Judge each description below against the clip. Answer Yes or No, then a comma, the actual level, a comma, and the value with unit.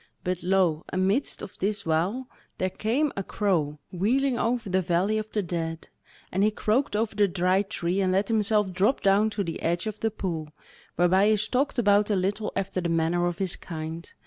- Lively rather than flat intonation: No, average, 3.4 semitones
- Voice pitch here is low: No, high, 195 Hz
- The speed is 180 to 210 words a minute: Yes, average, 200 wpm